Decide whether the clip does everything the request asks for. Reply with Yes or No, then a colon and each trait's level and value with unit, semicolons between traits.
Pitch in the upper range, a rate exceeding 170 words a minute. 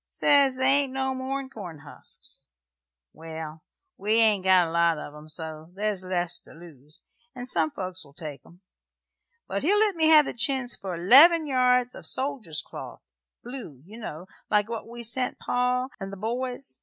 Yes: high, 215 Hz; average, 180 wpm